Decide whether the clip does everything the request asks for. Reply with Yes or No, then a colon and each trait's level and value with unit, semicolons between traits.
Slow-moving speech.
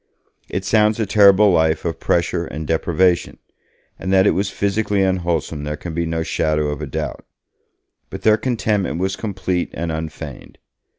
No: average, 165 wpm